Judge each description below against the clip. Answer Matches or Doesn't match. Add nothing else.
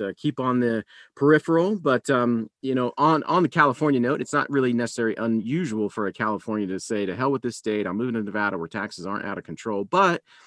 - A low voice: Matches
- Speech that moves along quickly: Matches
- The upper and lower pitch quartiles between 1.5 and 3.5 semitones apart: Doesn't match